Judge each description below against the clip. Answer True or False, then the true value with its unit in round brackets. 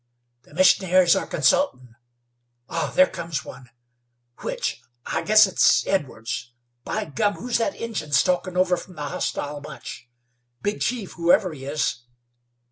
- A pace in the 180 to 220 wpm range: False (135 wpm)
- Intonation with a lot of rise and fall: True (5.7 semitones)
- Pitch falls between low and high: True (170 Hz)